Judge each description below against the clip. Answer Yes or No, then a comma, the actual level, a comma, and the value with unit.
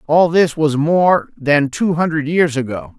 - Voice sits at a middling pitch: Yes, medium, 155 Hz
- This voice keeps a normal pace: Yes, average, 180 wpm